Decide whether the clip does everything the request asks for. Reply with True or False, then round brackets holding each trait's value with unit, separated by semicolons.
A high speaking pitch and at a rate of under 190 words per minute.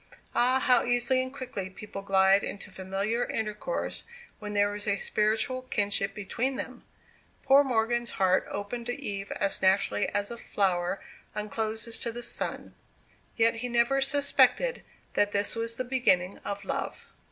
True (220 Hz; 150 wpm)